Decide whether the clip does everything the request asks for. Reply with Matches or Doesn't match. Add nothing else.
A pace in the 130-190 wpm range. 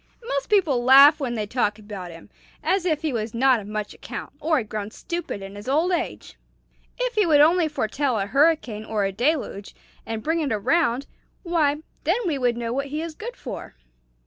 Doesn't match